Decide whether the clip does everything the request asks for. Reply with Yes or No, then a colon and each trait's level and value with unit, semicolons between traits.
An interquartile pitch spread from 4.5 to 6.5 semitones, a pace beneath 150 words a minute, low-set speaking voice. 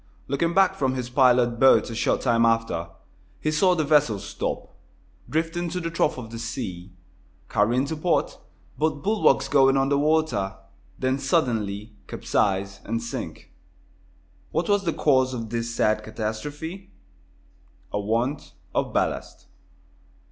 Yes: wide, 5.4 semitones; average, 140 wpm; low, 130 Hz